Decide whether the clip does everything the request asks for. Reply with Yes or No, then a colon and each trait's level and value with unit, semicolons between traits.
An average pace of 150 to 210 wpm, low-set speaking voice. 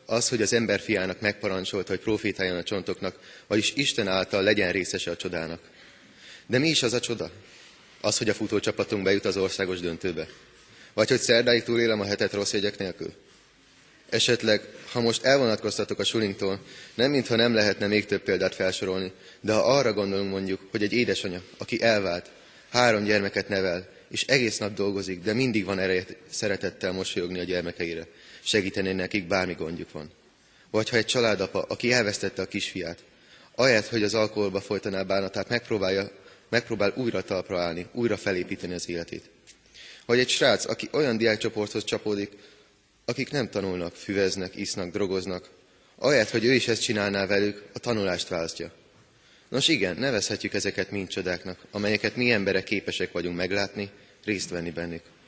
Yes: fast, 155 wpm; low, 100 Hz